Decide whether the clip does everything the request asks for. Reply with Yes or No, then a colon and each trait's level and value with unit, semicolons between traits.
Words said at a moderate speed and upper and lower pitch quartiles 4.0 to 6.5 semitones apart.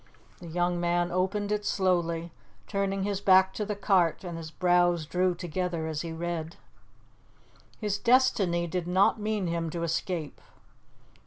No: average, 150 wpm; narrow, 2.5 semitones